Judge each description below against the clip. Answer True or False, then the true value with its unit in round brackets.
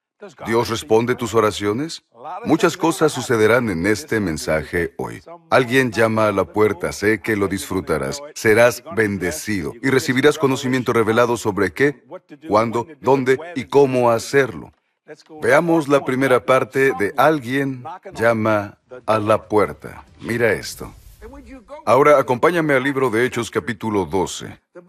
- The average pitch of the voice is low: True (125 Hz)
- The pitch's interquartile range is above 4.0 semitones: True (4.4 semitones)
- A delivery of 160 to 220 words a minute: False (130 wpm)